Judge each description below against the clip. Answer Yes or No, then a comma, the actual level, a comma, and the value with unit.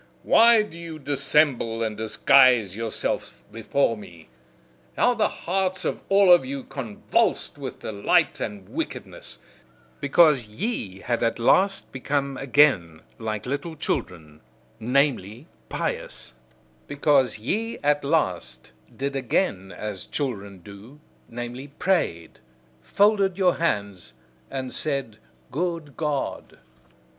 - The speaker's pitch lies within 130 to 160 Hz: Yes, low, 135 Hz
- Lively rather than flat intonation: Yes, wide, 6.5 semitones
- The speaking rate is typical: No, slow, 115 wpm